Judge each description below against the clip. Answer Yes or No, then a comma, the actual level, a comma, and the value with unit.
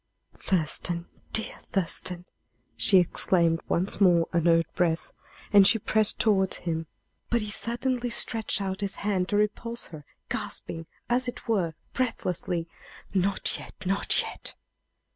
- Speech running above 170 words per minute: No, slow, 135 wpm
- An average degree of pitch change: Yes, average, 4.2 semitones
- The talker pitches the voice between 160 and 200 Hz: Yes, high, 190 Hz